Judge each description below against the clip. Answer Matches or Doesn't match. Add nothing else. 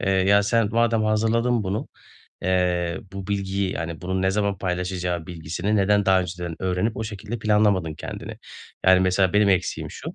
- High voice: Doesn't match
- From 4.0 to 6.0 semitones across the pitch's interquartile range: Doesn't match